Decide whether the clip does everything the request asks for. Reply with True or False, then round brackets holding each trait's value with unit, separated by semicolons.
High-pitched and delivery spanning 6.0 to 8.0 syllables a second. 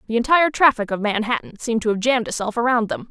True (230 Hz; 7.3 syllables/s)